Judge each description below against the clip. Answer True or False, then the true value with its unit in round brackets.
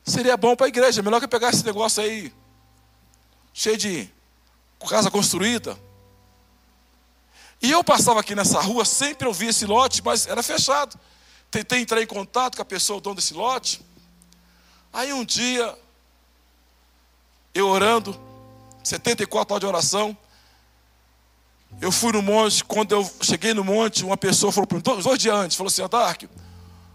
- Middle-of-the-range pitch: False (200 Hz)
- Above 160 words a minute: False (150 wpm)